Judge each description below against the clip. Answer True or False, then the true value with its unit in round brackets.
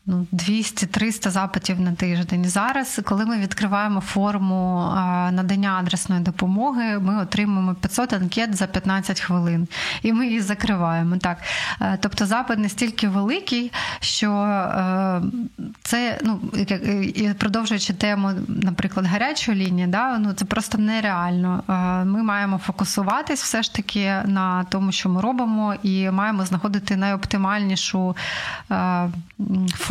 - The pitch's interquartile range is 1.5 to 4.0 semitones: True (2.5 semitones)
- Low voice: False (200 Hz)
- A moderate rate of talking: True (115 wpm)